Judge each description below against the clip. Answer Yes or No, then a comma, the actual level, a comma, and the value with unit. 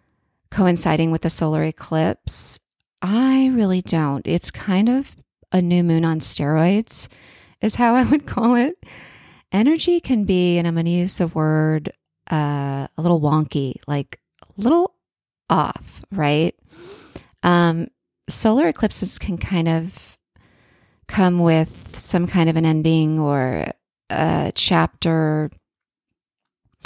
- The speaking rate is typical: No, slow, 125 wpm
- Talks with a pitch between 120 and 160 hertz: No, medium, 170 Hz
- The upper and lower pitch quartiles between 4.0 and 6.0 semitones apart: Yes, average, 4.6 semitones